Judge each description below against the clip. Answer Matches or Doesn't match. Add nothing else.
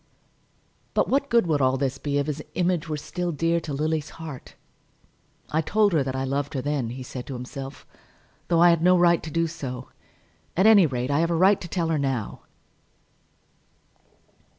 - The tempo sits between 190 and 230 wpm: Matches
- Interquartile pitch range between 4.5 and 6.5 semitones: Doesn't match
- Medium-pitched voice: Matches